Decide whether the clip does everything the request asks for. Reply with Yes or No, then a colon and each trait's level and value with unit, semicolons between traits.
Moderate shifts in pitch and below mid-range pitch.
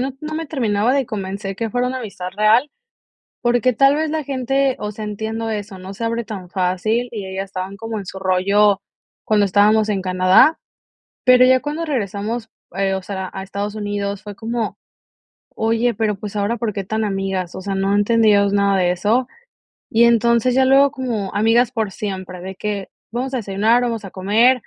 No: average, 3.5 semitones; high, 215 Hz